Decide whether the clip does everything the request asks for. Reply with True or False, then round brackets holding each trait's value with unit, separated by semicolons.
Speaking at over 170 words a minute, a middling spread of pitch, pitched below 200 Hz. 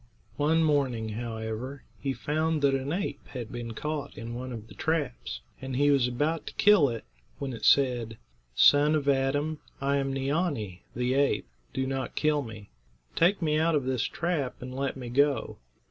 True (180 wpm; 3.4 semitones; 135 Hz)